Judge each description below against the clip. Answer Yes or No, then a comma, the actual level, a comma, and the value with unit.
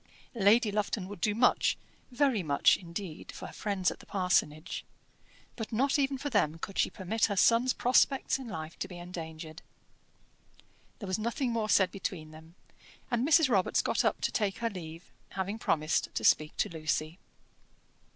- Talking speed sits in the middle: Yes, average, 170 wpm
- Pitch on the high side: Yes, high, 195 Hz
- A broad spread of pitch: Yes, wide, 5.7 semitones